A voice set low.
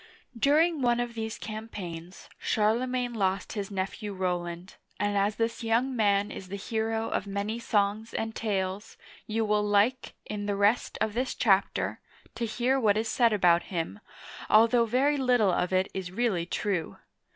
No: high, 215 Hz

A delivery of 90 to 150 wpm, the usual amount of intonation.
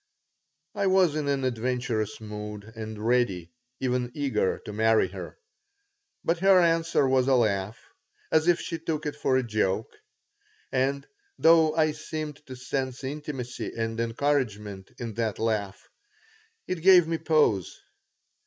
No: average, 140 wpm; wide, 5.8 semitones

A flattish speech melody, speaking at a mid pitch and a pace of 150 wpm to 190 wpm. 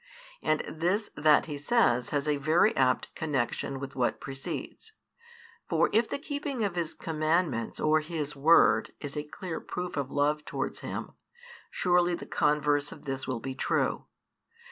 No: average, 3.9 semitones; medium, 150 Hz; average, 160 wpm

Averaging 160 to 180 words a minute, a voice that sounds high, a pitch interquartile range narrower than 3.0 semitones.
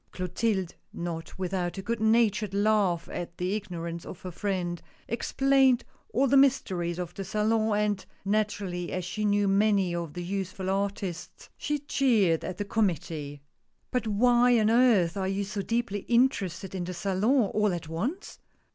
No: average, 165 wpm; high, 200 Hz; average, 3.7 semitones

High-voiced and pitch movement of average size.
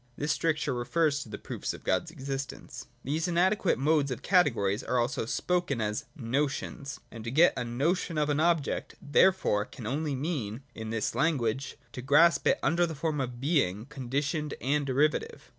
No: medium, 140 Hz; average, 4.6 semitones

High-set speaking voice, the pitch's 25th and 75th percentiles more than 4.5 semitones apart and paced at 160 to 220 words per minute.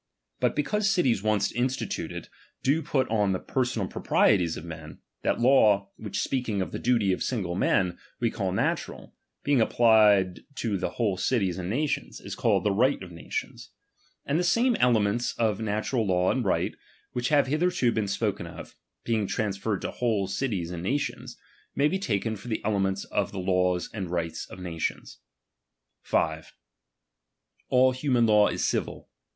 No: low, 105 Hz; average, 4.9 semitones; average, 165 wpm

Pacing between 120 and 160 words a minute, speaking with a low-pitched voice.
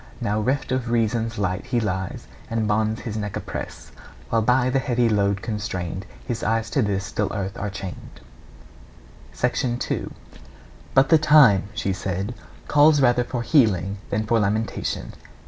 Yes: average, 150 wpm; low, 110 Hz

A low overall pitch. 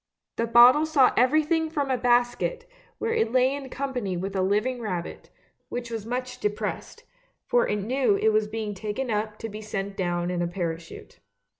No: high, 230 Hz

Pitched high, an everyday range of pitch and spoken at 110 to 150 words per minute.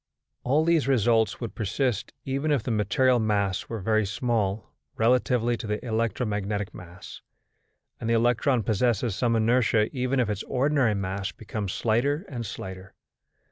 No: low, 115 Hz; average, 3.3 semitones; average, 145 wpm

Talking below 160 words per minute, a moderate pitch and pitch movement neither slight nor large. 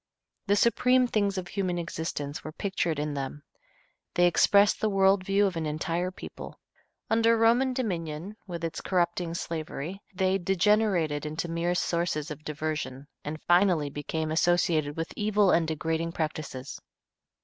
Yes: average, 145 wpm; medium, 170 Hz; average, 4.0 semitones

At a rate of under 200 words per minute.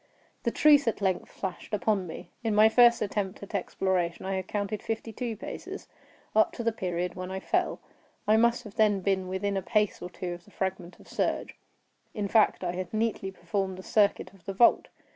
No: fast, 205 wpm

